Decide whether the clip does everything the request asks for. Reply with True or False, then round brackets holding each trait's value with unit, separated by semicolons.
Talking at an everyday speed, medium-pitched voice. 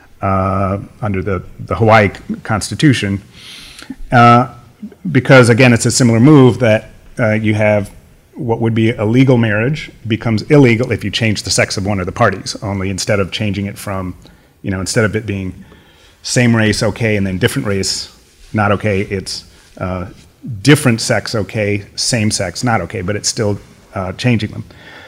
False (170 wpm; 105 Hz)